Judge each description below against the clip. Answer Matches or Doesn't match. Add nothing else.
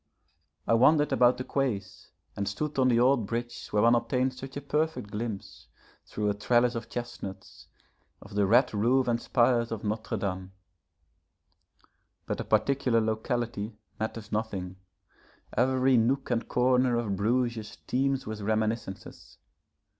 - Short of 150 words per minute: Matches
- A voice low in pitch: Matches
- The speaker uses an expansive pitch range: Doesn't match